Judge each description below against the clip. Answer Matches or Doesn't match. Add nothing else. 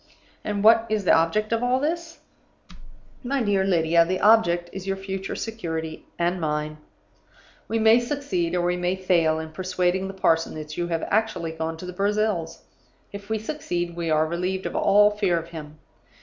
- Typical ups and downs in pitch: Matches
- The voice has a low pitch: Doesn't match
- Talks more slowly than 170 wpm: Doesn't match